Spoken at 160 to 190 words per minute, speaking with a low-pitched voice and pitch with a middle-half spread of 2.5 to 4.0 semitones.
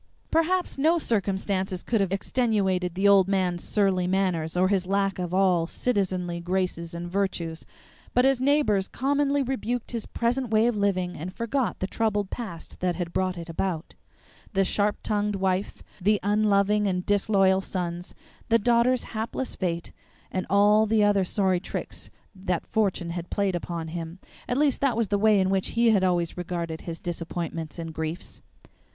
No: average, 170 wpm; high, 195 Hz; average, 3.4 semitones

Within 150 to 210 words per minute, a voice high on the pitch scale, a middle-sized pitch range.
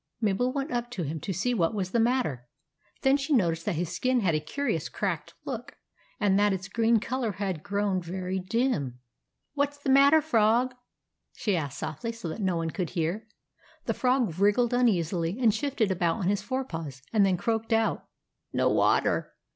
No: average, 195 wpm; high, 205 Hz; wide, 5.9 semitones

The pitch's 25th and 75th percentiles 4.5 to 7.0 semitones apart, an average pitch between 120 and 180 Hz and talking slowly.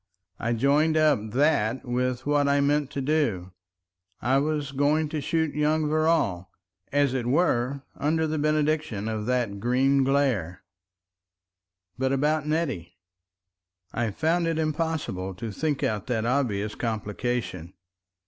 Yes: average, 4.8 semitones; medium, 140 Hz; slow, 130 wpm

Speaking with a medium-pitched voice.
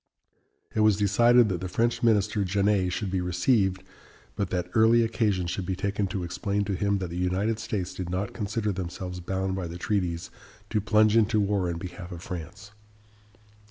No: low, 100 Hz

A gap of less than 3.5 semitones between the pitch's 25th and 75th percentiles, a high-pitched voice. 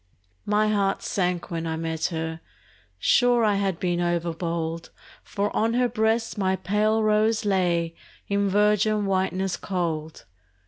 No: average, 3.8 semitones; high, 195 Hz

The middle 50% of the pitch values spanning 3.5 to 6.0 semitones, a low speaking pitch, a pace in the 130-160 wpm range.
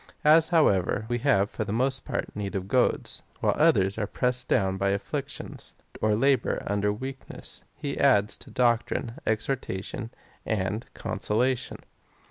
Yes: average, 4.2 semitones; low, 110 Hz; average, 145 wpm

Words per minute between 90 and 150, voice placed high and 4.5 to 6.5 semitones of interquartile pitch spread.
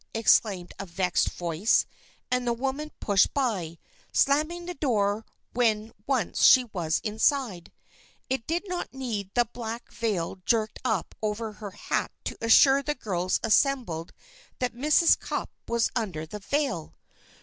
Yes: average, 140 wpm; high, 225 Hz; average, 5.0 semitones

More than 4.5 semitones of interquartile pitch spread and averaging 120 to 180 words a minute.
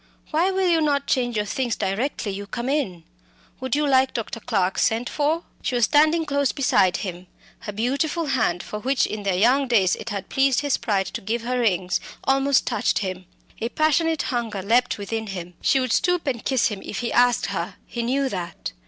No: wide, 5.4 semitones; fast, 205 wpm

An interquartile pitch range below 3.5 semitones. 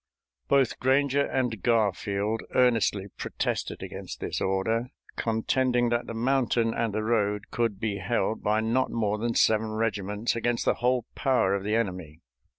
Yes: average, 2.7 semitones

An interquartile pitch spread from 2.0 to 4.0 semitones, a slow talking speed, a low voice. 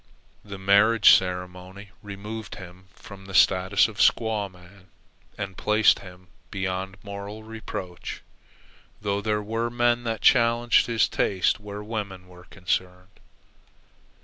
Yes: average, 2.8 semitones; slow, 120 wpm; low, 100 Hz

